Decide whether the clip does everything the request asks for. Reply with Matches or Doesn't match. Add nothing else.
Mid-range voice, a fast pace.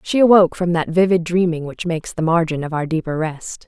Matches